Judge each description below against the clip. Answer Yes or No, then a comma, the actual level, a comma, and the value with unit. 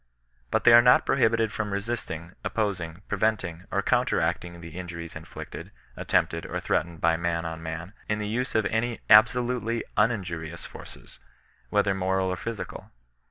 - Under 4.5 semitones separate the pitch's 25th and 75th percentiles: No, average, 4.9 semitones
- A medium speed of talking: Yes, average, 160 wpm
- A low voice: Yes, very low, 95 Hz